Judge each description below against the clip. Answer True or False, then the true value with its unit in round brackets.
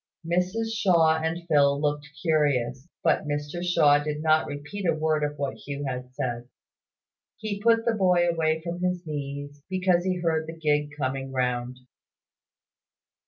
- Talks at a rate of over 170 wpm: False (155 wpm)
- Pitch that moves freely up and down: False (3.5 semitones)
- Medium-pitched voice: True (155 Hz)